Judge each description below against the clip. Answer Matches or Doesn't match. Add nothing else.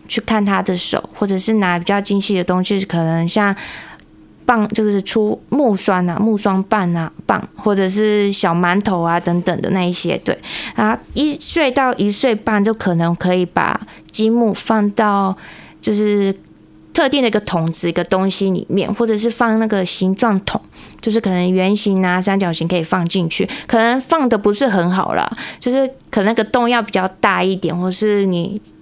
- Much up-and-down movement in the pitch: Doesn't match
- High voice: Matches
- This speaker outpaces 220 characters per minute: Matches